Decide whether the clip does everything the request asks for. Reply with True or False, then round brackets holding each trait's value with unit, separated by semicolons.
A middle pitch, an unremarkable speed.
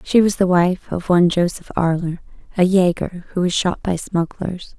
True (180 Hz; 190 wpm)